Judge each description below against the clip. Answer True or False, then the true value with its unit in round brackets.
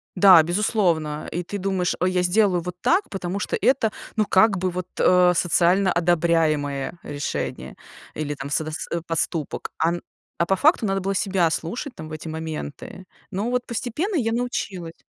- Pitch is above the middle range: False (180 Hz)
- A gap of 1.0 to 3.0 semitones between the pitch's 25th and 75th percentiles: False (3.7 semitones)